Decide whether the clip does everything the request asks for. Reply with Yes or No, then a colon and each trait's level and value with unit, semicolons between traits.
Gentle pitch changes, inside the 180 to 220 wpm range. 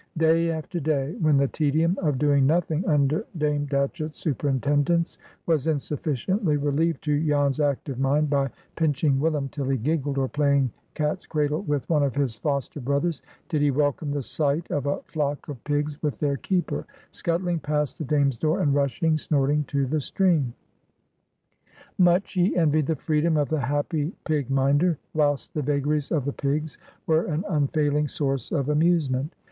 No: narrow, 2.1 semitones; average, 165 wpm